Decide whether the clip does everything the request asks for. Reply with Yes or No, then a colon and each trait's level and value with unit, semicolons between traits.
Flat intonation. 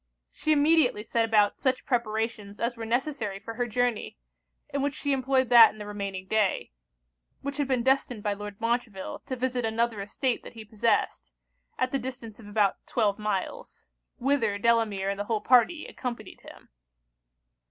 No: average, 3.6 semitones